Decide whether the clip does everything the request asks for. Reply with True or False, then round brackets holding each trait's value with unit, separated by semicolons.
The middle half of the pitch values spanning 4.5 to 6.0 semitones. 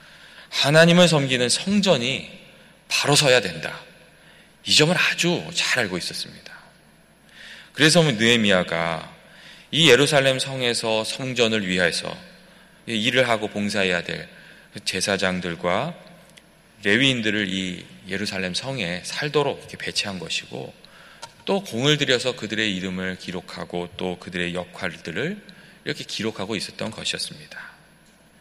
False (9.0 semitones)